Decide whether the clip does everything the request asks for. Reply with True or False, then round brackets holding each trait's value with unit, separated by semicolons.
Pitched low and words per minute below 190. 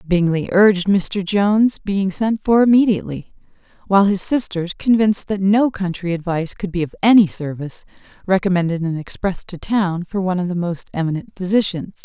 False (190 Hz; 165 wpm)